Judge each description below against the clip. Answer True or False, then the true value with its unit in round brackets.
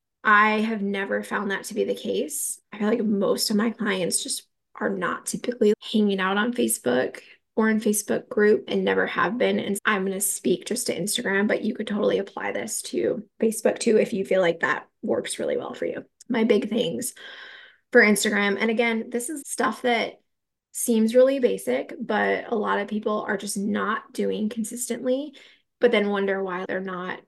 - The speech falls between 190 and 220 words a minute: True (195 wpm)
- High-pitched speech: True (215 Hz)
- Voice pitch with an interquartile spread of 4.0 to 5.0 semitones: False (2.8 semitones)